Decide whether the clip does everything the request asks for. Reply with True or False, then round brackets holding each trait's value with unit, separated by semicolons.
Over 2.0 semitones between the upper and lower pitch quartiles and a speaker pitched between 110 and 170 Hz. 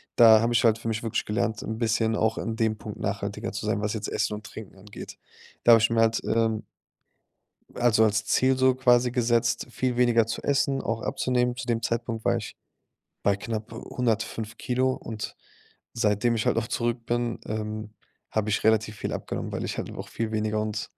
False (1.7 semitones; 115 Hz)